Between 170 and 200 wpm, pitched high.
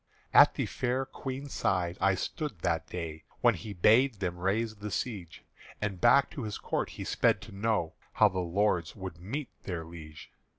No: average, 180 wpm; low, 100 Hz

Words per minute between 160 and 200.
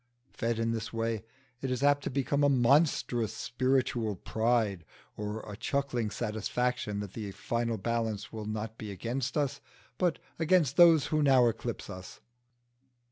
No: average, 150 wpm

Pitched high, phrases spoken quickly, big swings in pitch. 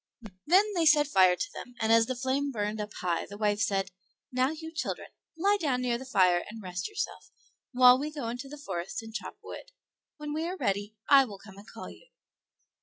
Yes: very high, 250 Hz; fast, 215 wpm; wide, 6.3 semitones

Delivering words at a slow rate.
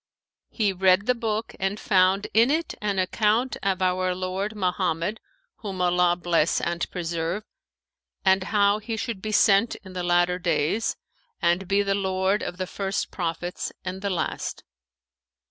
No: average, 155 wpm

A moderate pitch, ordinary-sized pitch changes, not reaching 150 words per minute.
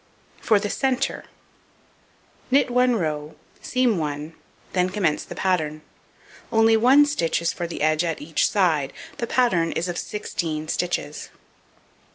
No: medium, 180 Hz; wide, 6.6 semitones; average, 140 wpm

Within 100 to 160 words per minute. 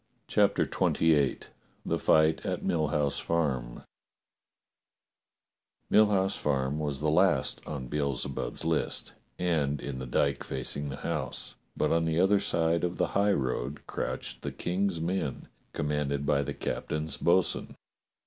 Yes: average, 140 wpm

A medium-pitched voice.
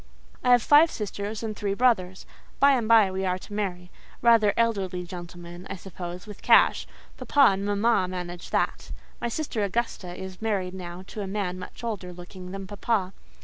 No: high, 195 Hz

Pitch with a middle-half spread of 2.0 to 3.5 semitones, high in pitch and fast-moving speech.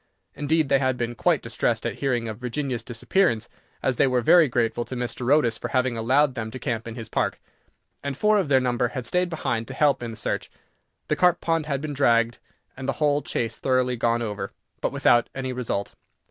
No: average, 3.2 semitones; low, 125 Hz; fast, 215 wpm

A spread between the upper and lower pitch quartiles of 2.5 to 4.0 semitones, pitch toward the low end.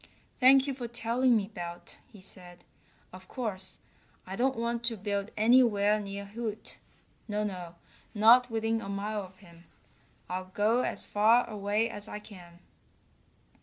No: average, 3.2 semitones; high, 210 Hz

